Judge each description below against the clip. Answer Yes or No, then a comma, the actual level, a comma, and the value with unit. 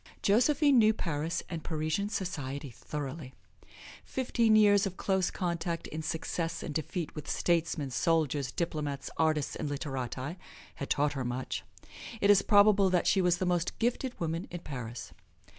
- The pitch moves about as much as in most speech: Yes, average, 4.9 semitones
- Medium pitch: Yes, medium, 165 Hz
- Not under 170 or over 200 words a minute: No, average, 150 wpm